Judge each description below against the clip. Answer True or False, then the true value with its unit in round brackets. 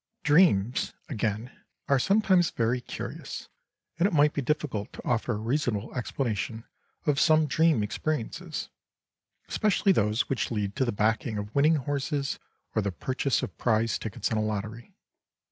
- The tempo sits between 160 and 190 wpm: False (150 wpm)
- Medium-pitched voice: False (125 Hz)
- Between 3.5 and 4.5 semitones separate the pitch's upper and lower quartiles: False (5.5 semitones)